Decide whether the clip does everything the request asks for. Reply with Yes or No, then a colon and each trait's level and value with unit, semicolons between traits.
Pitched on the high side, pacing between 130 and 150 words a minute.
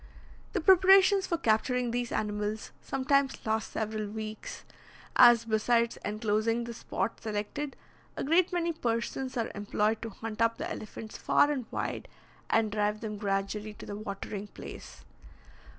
Yes: high, 225 Hz; average, 145 wpm